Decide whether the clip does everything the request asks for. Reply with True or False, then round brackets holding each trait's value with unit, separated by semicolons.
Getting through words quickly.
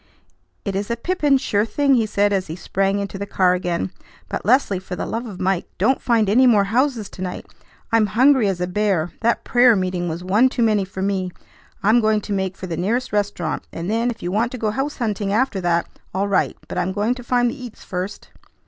True (230 wpm)